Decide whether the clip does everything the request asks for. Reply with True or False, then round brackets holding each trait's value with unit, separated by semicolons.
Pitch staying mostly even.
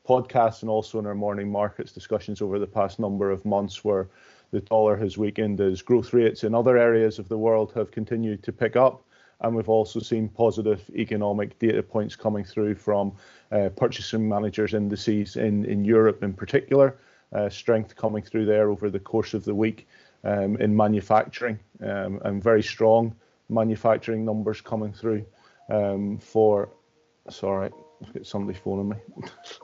True (1.5 semitones)